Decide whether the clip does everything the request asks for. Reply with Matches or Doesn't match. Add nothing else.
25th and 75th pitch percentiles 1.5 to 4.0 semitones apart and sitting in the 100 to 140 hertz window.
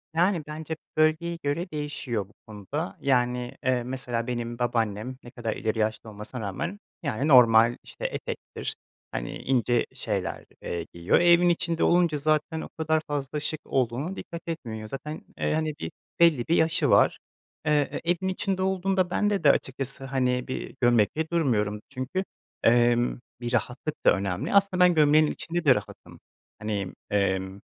Doesn't match